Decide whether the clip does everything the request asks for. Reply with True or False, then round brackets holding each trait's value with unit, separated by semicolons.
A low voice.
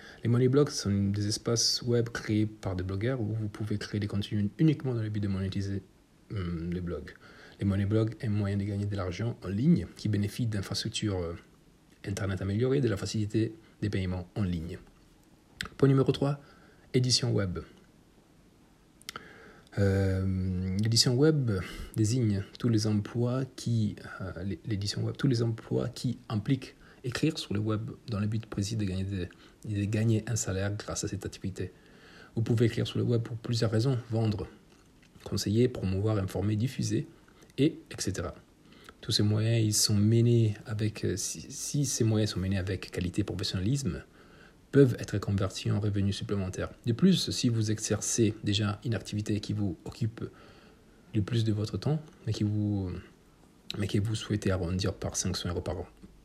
True (105 Hz)